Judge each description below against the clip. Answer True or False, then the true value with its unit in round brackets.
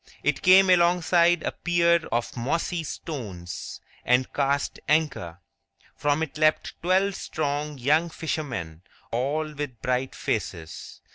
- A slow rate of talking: True (120 wpm)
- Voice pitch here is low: False (150 Hz)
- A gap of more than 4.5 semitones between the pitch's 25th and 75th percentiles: True (5.0 semitones)